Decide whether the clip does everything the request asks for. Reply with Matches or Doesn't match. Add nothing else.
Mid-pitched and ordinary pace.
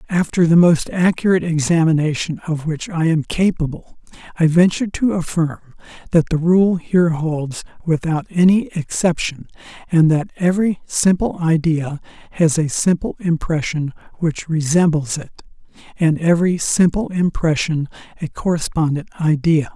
Doesn't match